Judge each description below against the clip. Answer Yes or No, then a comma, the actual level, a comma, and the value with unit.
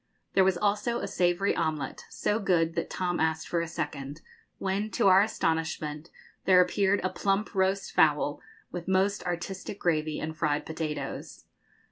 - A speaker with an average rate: Yes, average, 155 wpm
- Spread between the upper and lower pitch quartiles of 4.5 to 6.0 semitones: No, average, 3.6 semitones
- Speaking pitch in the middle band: Yes, medium, 175 Hz